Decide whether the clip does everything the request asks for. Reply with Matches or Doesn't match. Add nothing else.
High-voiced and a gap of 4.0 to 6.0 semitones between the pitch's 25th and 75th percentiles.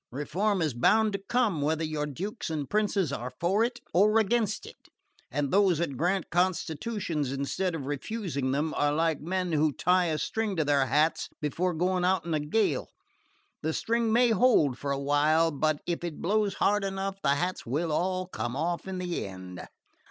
Doesn't match